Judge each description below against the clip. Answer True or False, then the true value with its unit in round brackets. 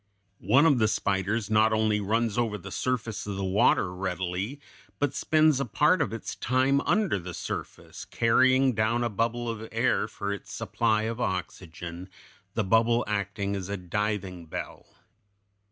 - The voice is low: True (110 Hz)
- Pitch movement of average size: True (3.5 semitones)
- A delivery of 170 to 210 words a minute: False (160 wpm)